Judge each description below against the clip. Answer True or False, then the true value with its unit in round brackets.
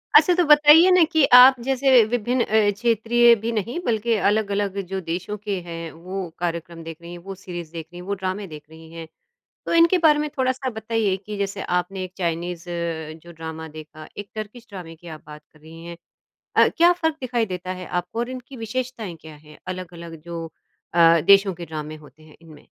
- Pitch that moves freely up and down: True (6.2 semitones)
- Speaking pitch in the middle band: False (195 Hz)